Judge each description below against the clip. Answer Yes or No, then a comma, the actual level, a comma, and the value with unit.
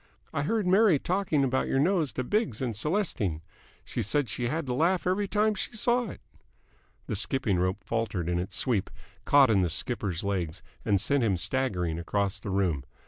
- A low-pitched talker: Yes, low, 125 Hz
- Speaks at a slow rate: No, average, 190 wpm